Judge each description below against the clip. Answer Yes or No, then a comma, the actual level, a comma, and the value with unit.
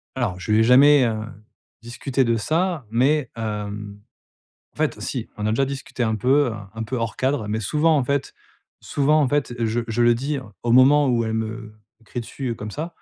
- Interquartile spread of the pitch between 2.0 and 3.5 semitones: No, average, 4.1 semitones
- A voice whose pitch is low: Yes, low, 120 Hz